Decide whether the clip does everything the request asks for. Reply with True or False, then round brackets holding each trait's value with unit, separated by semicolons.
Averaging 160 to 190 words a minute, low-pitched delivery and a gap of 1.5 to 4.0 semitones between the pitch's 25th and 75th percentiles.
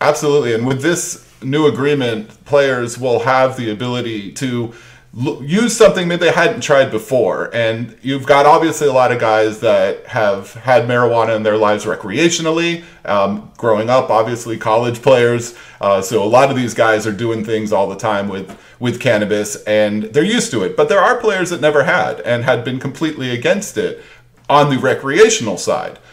False (185 wpm; 125 Hz; 5.2 semitones)